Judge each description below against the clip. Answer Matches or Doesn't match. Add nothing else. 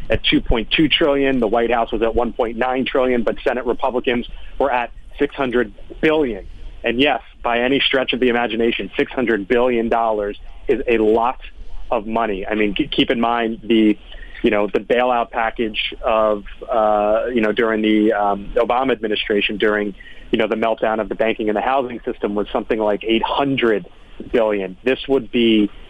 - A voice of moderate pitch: Doesn't match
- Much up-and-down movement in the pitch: Doesn't match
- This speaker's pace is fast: Doesn't match